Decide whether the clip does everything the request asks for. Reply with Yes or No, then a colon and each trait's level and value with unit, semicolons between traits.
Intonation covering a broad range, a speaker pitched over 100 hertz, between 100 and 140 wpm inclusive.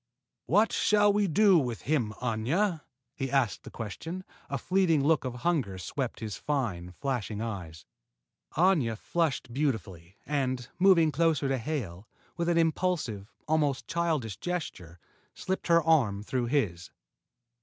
Yes: wide, 7.1 semitones; medium, 140 Hz; slow, 135 wpm